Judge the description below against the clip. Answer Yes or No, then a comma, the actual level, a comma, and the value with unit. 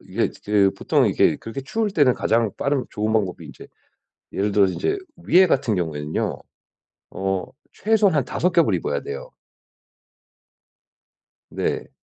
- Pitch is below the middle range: Yes, low, 125 Hz